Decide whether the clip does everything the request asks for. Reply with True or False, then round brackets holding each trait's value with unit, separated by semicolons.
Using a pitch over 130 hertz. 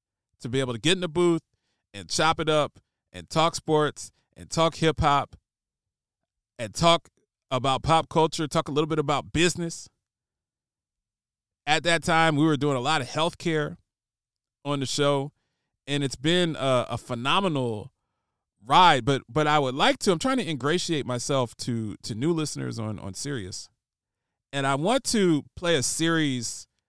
True (140 Hz)